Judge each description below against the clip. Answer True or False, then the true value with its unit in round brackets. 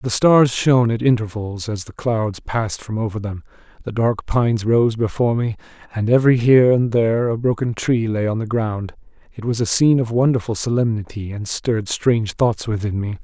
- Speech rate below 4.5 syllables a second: False (5.5 syllables/s)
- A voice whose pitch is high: False (115 Hz)